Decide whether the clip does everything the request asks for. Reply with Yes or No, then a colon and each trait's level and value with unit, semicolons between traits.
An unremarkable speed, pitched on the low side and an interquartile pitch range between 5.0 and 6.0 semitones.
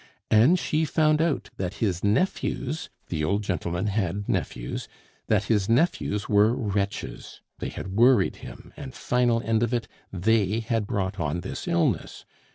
No: average, 155 wpm; low, 105 Hz; average, 4.0 semitones